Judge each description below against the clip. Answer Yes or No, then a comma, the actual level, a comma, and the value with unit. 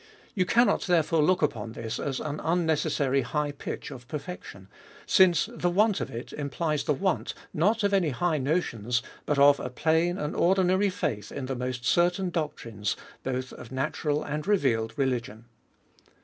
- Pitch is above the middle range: No, medium, 150 Hz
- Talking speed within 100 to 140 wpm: No, average, 175 wpm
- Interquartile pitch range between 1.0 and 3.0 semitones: No, wide, 5.5 semitones